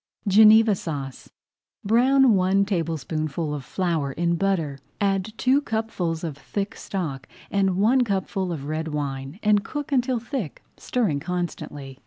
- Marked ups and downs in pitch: Yes, wide, 5.9 semitones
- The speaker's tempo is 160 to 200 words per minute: No, slow, 135 wpm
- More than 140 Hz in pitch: Yes, medium, 185 Hz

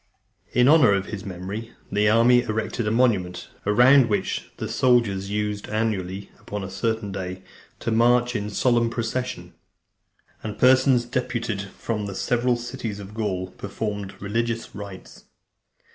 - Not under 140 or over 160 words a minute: Yes, average, 145 wpm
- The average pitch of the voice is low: Yes, low, 110 Hz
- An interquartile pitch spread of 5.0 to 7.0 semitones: No, average, 3.0 semitones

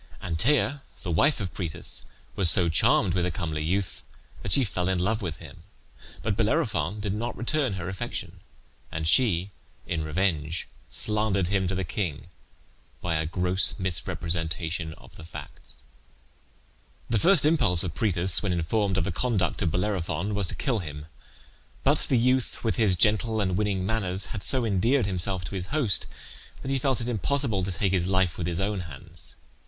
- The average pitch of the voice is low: Yes, very low, 95 Hz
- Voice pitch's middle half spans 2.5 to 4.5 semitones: Yes, average, 4.2 semitones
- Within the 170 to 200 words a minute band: Yes, average, 175 wpm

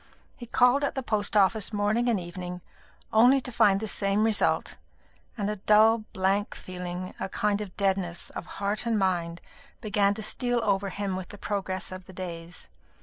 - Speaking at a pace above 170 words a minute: Yes, average, 180 wpm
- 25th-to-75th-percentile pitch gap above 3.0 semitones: No, narrow, 2.6 semitones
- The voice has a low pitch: No, high, 200 Hz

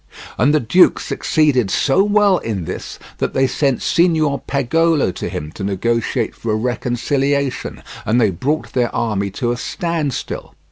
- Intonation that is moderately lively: Yes, average, 5.0 semitones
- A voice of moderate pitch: No, low, 130 Hz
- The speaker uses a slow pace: No, average, 155 wpm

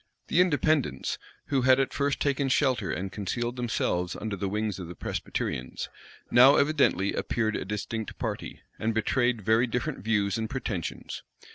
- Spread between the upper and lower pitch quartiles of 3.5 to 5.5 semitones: Yes, average, 4.8 semitones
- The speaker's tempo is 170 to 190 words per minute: No, average, 155 wpm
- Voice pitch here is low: Yes, low, 115 Hz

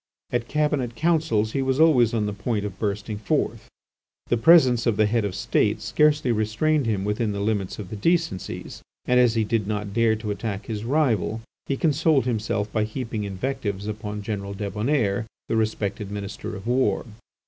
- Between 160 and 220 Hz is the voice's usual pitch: No, low, 110 Hz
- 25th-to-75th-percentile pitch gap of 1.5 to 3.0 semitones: No, average, 3.7 semitones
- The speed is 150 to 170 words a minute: No, average, 180 wpm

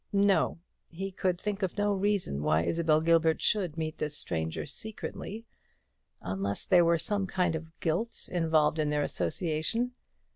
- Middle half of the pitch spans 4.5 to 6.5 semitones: No, average, 4.1 semitones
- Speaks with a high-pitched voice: No, medium, 165 Hz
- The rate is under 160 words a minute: Yes, average, 150 wpm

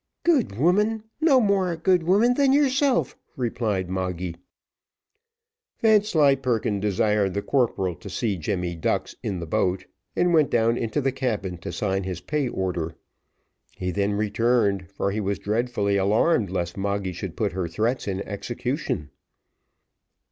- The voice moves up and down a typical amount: No, wide, 8.0 semitones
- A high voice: No, low, 105 Hz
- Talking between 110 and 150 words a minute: Yes, average, 145 wpm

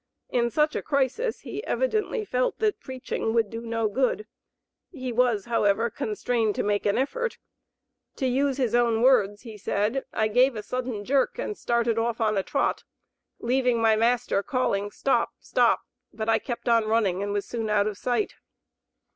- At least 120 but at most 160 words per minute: No, average, 175 wpm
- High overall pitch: Yes, high, 235 Hz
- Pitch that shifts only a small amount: No, average, 3.3 semitones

